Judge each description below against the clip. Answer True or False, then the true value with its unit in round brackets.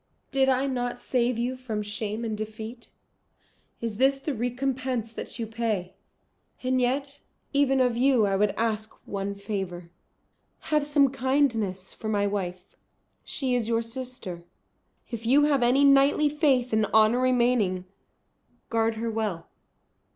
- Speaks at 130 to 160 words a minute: True (145 wpm)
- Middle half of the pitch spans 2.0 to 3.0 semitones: False (3.5 semitones)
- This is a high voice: True (235 Hz)